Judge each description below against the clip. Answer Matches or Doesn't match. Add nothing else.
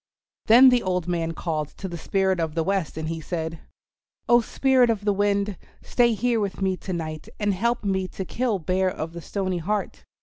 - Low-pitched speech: Doesn't match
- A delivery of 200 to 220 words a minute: Matches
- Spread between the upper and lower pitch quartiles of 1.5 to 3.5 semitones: Doesn't match